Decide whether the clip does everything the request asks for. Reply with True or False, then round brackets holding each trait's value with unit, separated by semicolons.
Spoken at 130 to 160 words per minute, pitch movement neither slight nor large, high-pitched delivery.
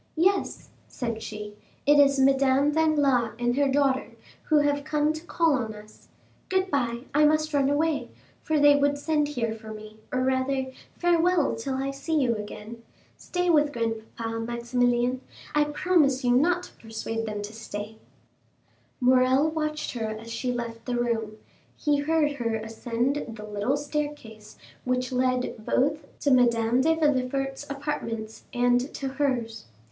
True (155 wpm; 4.2 semitones; 260 Hz)